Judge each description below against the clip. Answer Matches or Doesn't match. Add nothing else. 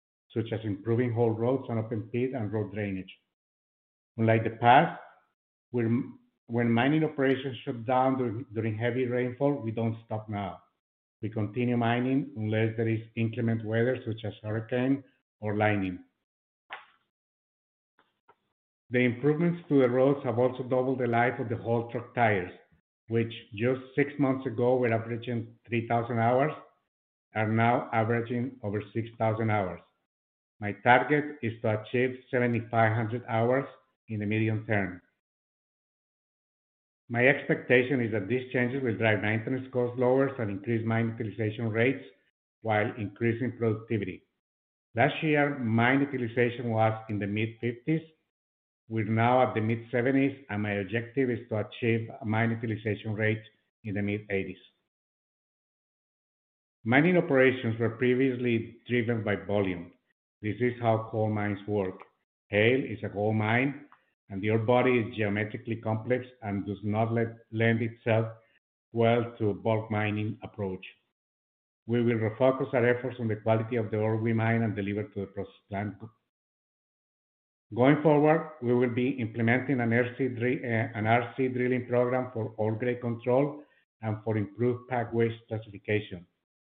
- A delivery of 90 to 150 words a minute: Matches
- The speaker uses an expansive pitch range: Doesn't match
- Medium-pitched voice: Doesn't match